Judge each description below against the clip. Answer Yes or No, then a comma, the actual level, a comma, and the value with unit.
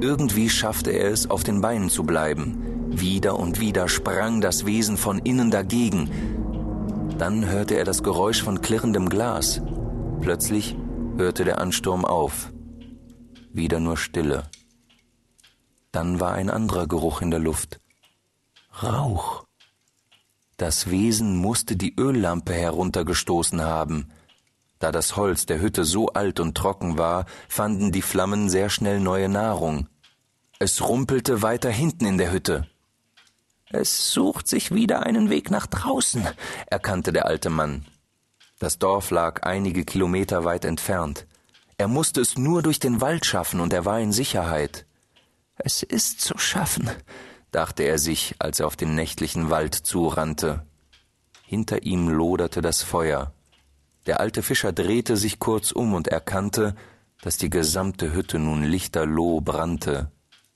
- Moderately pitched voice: No, very low, 95 Hz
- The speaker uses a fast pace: No, average, 140 wpm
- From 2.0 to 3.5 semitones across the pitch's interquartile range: No, average, 5.0 semitones